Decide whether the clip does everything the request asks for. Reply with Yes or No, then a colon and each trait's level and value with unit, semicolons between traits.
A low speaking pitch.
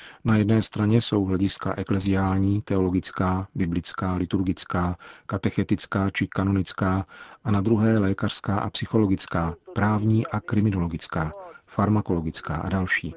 Yes: very low, 95 Hz